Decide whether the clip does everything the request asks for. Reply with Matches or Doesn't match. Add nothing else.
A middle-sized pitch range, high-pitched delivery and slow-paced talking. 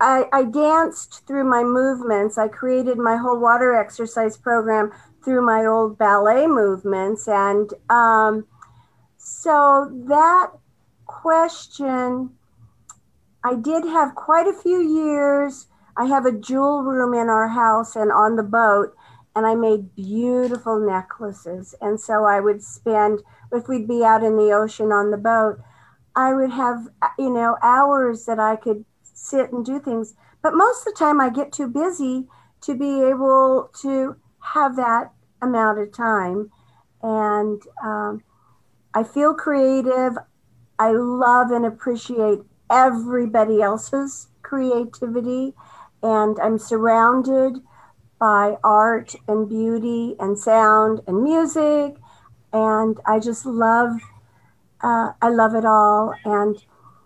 Matches